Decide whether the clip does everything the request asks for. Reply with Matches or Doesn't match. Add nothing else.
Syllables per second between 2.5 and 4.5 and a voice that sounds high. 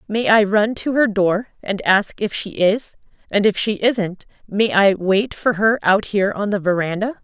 Matches